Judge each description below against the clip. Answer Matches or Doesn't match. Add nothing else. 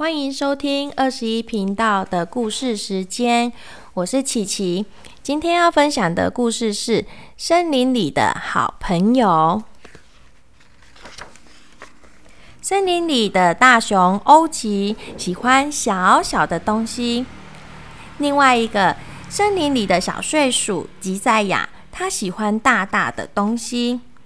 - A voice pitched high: Matches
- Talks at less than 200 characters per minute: Matches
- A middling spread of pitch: Matches